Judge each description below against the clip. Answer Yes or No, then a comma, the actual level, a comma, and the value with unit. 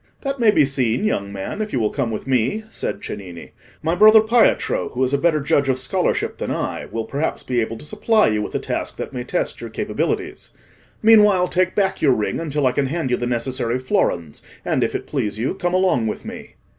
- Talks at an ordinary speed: No, fast, 225 wpm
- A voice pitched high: No, low, 135 Hz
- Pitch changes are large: Yes, wide, 8.1 semitones